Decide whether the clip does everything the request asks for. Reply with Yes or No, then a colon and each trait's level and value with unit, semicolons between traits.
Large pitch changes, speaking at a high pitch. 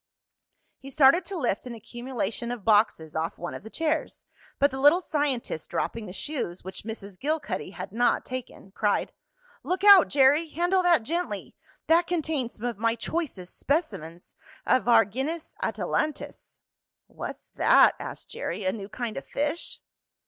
Yes: wide, 6.6 semitones; very high, 255 Hz